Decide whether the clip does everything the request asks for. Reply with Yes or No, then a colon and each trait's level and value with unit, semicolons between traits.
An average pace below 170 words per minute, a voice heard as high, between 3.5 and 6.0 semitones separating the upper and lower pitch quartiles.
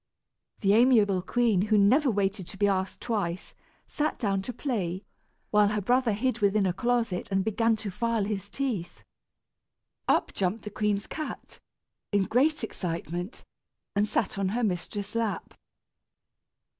No: average, 145 wpm; high, 205 Hz; average, 3.0 semitones